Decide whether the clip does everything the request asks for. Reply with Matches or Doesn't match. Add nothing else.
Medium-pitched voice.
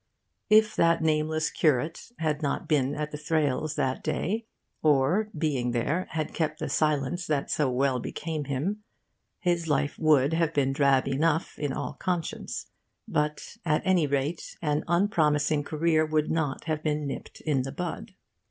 Matches